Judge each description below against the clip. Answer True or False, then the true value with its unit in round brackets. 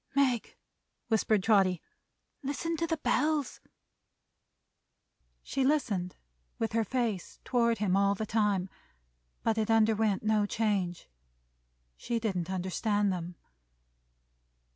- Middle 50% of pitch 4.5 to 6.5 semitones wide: False (3.4 semitones)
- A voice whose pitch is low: False (215 Hz)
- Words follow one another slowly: True (105 wpm)